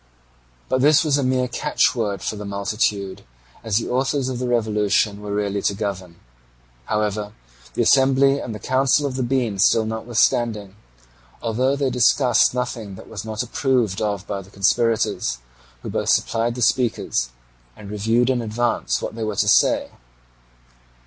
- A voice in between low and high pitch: No, low, 115 Hz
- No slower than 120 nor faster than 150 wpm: No, average, 160 wpm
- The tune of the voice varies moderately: Yes, average, 3.6 semitones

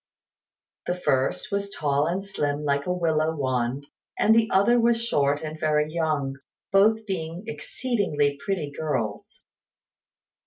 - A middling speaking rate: No, slow, 125 wpm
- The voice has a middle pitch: Yes, medium, 160 Hz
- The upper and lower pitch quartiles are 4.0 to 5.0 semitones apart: No, wide, 5.5 semitones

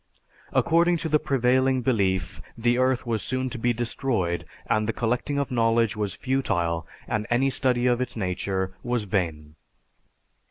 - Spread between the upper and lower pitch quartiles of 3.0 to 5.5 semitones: Yes, average, 4.6 semitones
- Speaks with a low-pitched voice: Yes, low, 120 Hz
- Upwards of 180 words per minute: No, average, 155 wpm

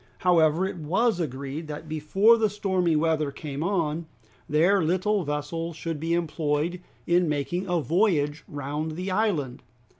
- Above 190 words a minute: No, average, 145 wpm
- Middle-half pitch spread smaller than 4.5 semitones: Yes, average, 3.4 semitones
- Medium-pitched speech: Yes, medium, 165 Hz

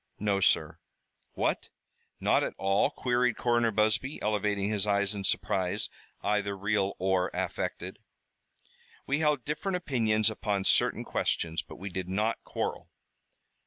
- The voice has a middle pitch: No, low, 105 Hz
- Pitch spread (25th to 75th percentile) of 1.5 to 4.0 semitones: Yes, average, 3.2 semitones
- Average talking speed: No, slow, 130 wpm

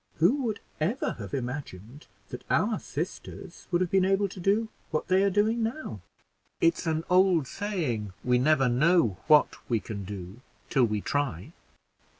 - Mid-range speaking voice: Yes, medium, 155 Hz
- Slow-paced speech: No, average, 160 wpm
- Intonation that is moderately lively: No, wide, 8.0 semitones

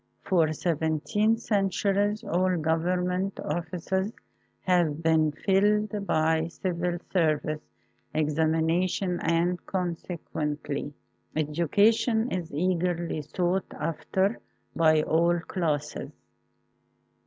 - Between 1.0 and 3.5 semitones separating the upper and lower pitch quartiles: Yes, average, 3.1 semitones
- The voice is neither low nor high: Yes, medium, 175 Hz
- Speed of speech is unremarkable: No, slow, 85 wpm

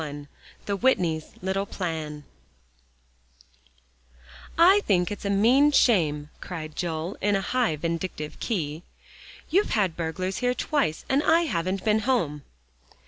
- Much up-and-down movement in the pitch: Yes, wide, 6.5 semitones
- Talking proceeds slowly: Yes, slow, 130 wpm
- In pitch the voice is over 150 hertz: Yes, medium, 185 Hz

